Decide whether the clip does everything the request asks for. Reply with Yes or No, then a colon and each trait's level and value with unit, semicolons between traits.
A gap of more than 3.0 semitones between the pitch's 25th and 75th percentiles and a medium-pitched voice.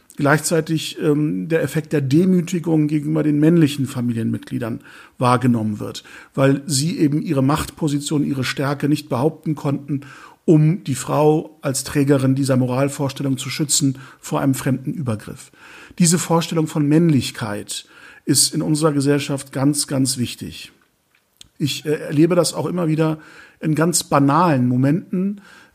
No: average, 2.7 semitones; medium, 145 Hz